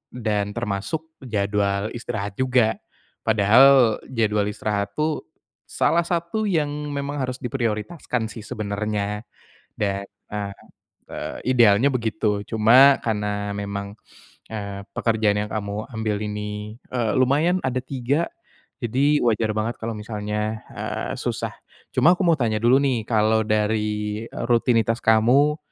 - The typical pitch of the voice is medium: No, low, 110 Hz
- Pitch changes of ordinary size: Yes, average, 3.5 semitones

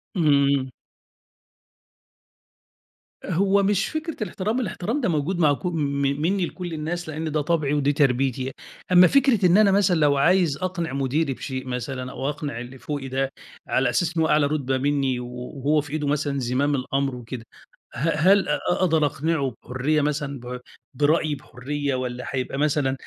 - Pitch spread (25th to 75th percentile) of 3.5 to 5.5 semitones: Yes, average, 4.1 semitones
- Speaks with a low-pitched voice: No, medium, 145 Hz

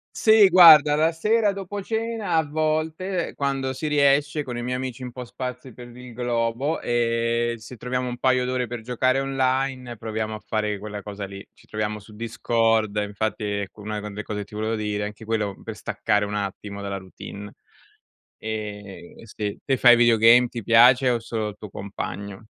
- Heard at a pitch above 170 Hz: No, low, 120 Hz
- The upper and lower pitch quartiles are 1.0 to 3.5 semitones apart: No, average, 3.9 semitones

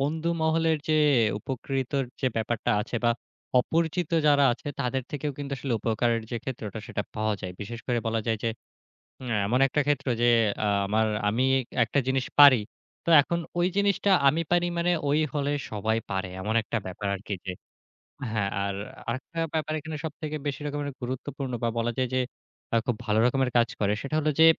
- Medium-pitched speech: No, low, 130 Hz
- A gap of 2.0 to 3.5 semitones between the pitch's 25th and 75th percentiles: No, average, 4.7 semitones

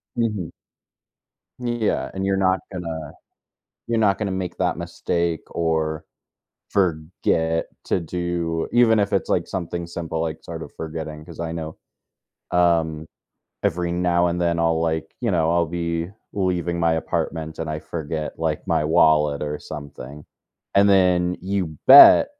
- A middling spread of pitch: No, narrow, 2.3 semitones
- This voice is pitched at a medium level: No, very low, 85 Hz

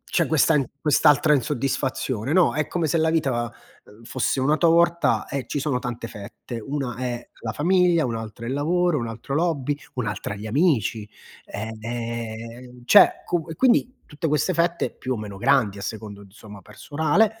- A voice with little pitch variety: No, wide, 5.6 semitones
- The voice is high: No, low, 130 Hz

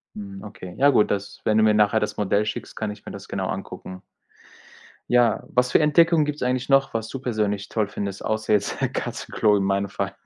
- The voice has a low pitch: Yes, low, 105 Hz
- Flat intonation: No, average, 3.7 semitones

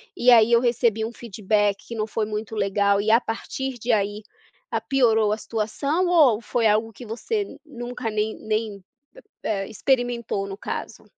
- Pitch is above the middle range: Yes, high, 225 Hz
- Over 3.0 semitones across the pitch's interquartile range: No, narrow, 2.4 semitones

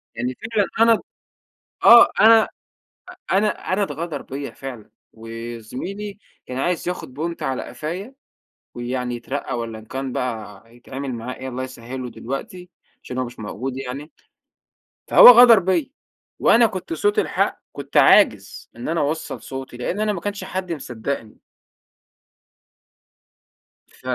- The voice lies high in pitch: No, medium, 140 Hz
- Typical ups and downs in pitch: No, wide, 7.5 semitones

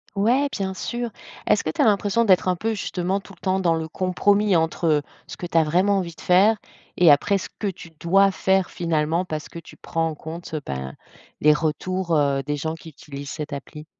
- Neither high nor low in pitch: Yes, medium, 175 Hz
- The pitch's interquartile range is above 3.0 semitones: Yes, average, 3.7 semitones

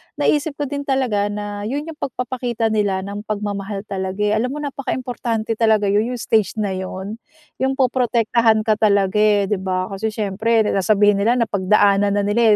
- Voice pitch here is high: Yes, high, 215 Hz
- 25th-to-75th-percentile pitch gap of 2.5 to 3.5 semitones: Yes, average, 2.8 semitones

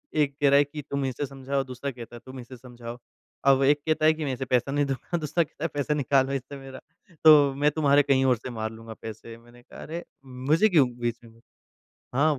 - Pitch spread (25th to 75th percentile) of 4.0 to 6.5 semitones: No, average, 2.8 semitones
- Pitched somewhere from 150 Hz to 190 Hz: No, low, 135 Hz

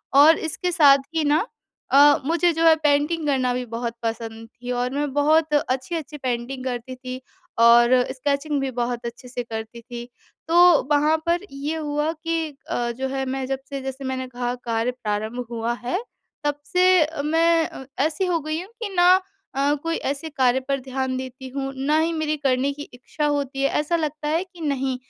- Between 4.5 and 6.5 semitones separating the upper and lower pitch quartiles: No, average, 3.8 semitones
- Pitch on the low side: No, very high, 275 Hz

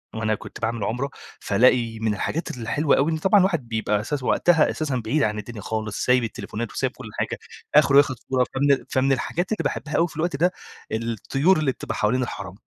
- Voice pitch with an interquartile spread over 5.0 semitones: Yes, wide, 5.4 semitones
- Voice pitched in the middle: No, low, 130 Hz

